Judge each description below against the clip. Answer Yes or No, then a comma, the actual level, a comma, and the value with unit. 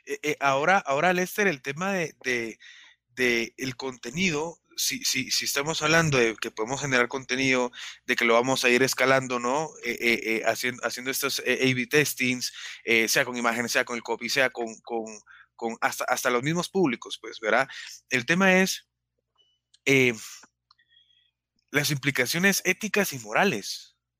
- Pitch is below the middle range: Yes, low, 130 Hz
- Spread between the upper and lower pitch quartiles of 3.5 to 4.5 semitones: Yes, average, 4.1 semitones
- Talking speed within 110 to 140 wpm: No, average, 155 wpm